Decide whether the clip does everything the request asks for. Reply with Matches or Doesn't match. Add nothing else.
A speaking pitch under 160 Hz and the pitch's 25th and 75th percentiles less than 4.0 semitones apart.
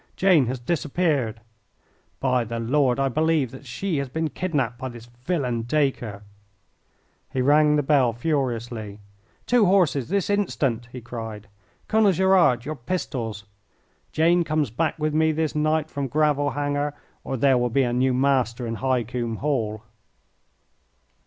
Doesn't match